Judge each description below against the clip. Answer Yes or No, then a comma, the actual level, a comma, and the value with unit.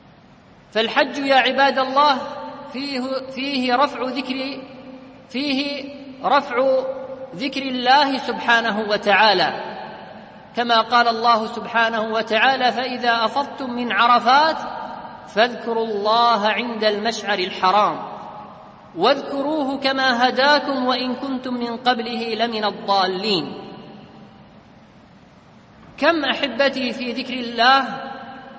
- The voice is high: Yes, very high, 255 Hz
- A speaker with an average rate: Yes, average, 90 wpm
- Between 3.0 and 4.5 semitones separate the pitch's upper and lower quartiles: No, narrow, 2.6 semitones